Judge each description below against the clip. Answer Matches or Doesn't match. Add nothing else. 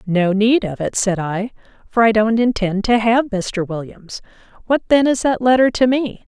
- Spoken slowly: Doesn't match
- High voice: Matches